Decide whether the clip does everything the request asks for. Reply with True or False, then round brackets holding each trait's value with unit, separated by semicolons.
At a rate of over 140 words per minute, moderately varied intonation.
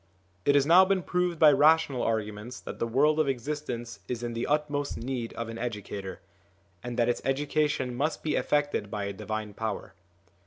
True (185 wpm; 4.7 semitones)